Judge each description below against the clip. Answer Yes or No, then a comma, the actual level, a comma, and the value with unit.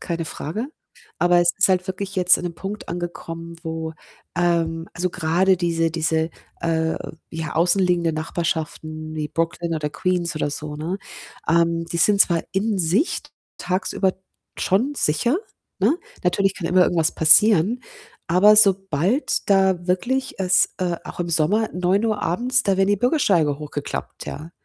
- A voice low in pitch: No, medium, 175 Hz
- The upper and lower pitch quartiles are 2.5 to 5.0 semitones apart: Yes, average, 2.9 semitones